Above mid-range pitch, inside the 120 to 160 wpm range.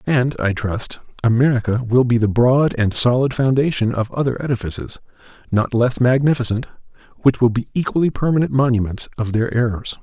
No: low, 120 Hz; average, 155 wpm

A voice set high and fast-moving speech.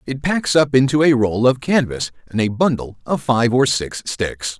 No: low, 125 Hz; fast, 210 wpm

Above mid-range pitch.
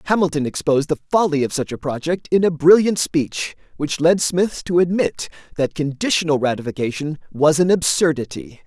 No: medium, 160 Hz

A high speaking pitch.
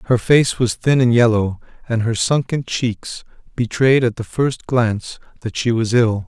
No: low, 115 Hz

